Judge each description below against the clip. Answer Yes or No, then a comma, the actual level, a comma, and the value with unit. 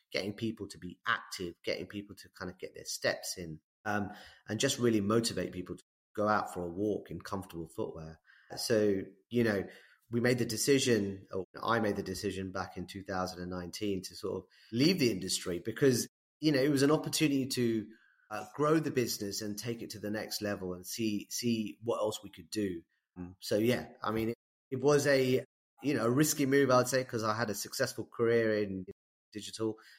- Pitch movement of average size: Yes, average, 4.0 semitones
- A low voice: Yes, low, 105 Hz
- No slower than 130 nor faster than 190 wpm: No, average, 200 wpm